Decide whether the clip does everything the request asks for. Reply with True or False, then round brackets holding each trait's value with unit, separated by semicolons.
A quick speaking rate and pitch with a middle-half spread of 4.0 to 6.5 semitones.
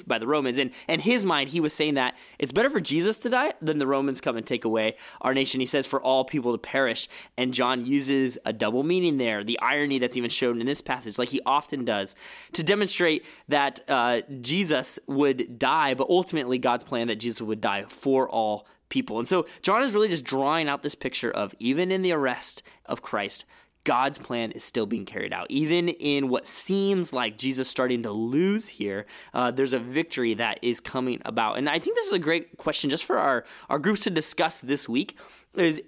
True (215 wpm; 4.8 semitones)